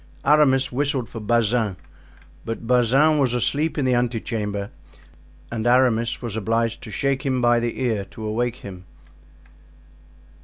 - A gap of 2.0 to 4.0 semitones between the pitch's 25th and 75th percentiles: Yes, narrow, 2.6 semitones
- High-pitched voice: No, low, 120 Hz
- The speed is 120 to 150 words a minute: Yes, average, 145 wpm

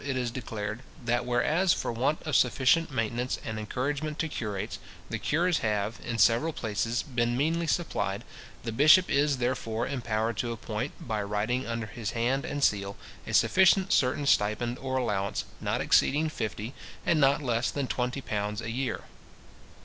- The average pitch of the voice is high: No, low, 120 Hz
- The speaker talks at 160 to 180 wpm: Yes, average, 165 wpm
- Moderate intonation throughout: Yes, average, 4.1 semitones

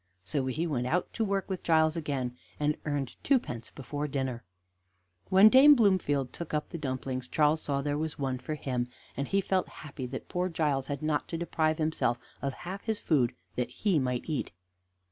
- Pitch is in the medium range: Yes, medium, 150 Hz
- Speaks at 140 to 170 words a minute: No, average, 190 wpm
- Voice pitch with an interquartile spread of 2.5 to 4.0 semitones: No, average, 4.4 semitones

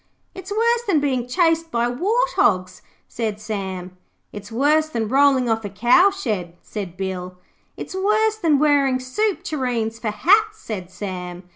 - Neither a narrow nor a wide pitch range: No, wide, 9.0 semitones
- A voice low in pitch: No, very high, 250 Hz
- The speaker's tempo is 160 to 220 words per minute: No, average, 150 wpm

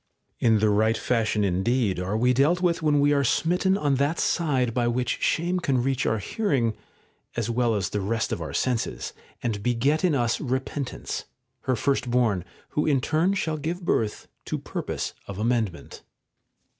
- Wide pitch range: No, average, 4.8 semitones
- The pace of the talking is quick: No, average, 175 wpm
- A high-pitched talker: No, low, 125 Hz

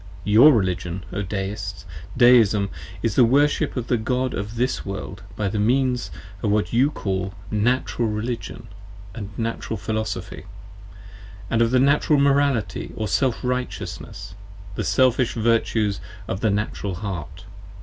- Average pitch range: Yes, average, 3.9 semitones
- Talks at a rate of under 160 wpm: Yes, average, 140 wpm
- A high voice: No, low, 110 Hz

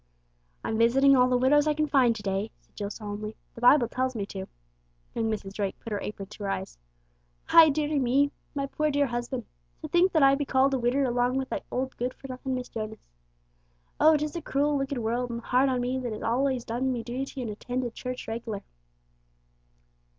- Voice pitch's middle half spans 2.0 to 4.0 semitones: Yes, average, 3.2 semitones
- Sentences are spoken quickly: Yes, fast, 210 wpm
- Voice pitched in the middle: No, very high, 250 Hz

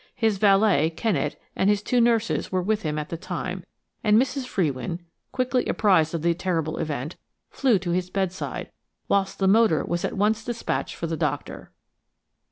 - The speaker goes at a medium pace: Yes, average, 175 wpm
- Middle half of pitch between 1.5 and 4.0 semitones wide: No, average, 4.7 semitones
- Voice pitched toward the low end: No, high, 190 Hz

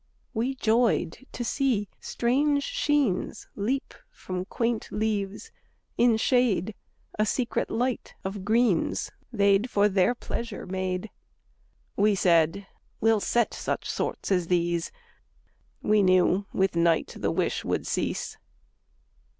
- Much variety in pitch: No, average, 4.3 semitones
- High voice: Yes, high, 210 Hz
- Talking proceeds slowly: Yes, slow, 120 wpm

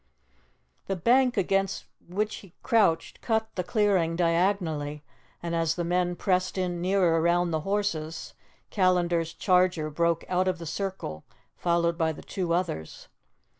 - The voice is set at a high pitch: No, medium, 175 Hz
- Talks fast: No, average, 140 wpm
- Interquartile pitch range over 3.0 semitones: No, narrow, 2.6 semitones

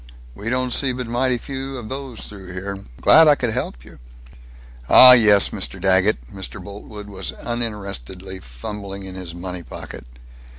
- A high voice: No, low, 100 Hz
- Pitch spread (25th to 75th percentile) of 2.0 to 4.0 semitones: No, average, 4.6 semitones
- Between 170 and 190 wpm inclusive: No, average, 160 wpm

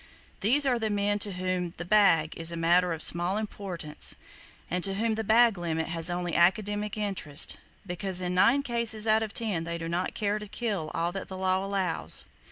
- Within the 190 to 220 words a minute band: Yes, average, 200 wpm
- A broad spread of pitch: No, average, 3.6 semitones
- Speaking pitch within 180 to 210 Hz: Yes, high, 190 Hz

